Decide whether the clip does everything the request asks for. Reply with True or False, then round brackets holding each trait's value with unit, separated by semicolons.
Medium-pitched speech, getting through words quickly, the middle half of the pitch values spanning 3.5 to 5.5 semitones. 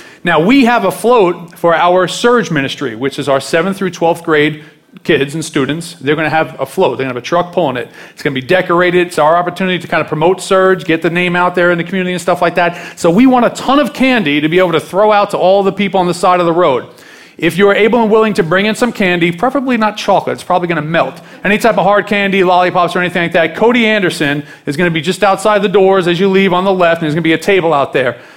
False (180 Hz; 285 wpm; 3.1 semitones)